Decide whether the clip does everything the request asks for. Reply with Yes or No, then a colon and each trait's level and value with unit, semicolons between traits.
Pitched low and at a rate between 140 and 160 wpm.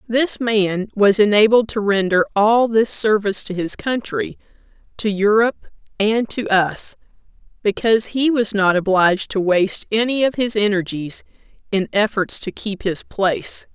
No: high, 210 Hz; average, 150 wpm